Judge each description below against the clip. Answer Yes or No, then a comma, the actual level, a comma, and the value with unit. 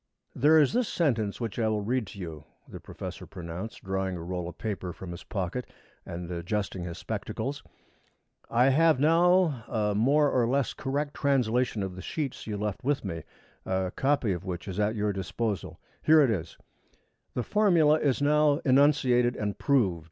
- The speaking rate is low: No, average, 175 wpm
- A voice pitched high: No, low, 115 Hz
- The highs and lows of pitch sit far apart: Yes, wide, 7.0 semitones